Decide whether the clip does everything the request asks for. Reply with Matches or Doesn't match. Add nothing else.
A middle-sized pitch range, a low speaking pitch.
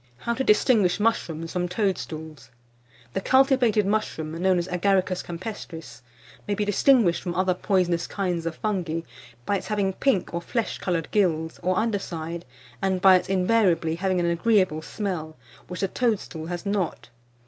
Doesn't match